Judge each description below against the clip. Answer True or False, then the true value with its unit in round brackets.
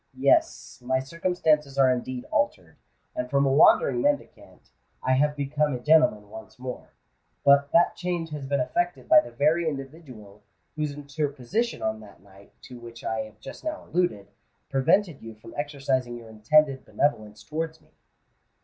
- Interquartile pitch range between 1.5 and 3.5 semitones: False (4.4 semitones)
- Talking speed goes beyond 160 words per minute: False (155 wpm)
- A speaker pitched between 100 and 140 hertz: True (135 Hz)